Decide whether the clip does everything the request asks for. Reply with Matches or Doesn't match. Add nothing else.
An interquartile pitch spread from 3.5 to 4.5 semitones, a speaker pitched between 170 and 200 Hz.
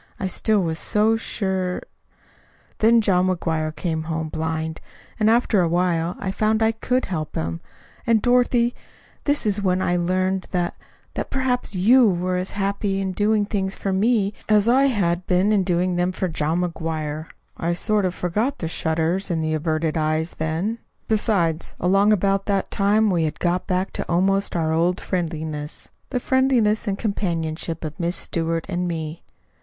Matches